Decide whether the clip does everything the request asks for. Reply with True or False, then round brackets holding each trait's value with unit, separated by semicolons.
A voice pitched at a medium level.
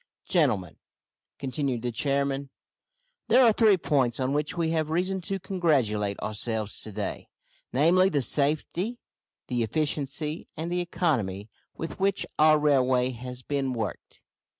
True (145 Hz)